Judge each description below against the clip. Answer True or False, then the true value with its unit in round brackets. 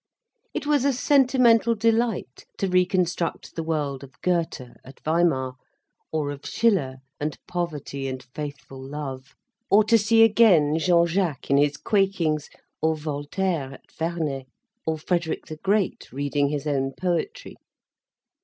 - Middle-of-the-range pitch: True (160 Hz)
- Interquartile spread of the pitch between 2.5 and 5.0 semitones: False (5.4 semitones)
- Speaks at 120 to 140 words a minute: True (135 wpm)